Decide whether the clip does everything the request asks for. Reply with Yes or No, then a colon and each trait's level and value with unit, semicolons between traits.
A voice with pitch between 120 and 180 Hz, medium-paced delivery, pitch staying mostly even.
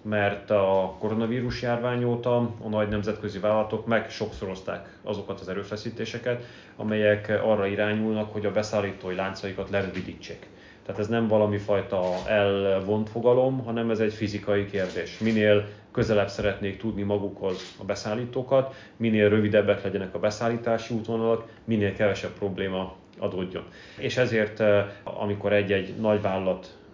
No: low, 105 Hz; average, 125 wpm; narrow, 2.0 semitones